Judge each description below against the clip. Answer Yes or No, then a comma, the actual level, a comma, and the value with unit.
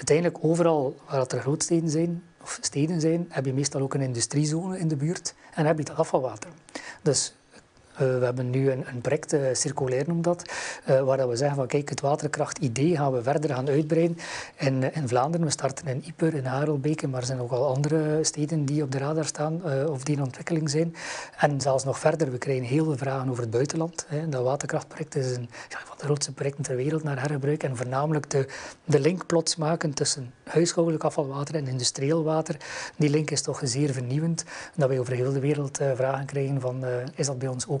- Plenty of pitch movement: No, average, 2.9 semitones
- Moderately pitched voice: Yes, medium, 145 Hz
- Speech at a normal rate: No, fast, 215 wpm